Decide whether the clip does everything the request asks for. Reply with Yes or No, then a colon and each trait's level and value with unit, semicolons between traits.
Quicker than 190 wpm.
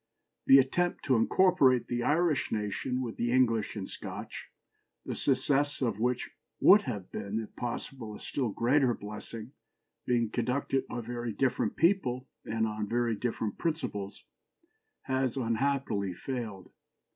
No: slow, 135 wpm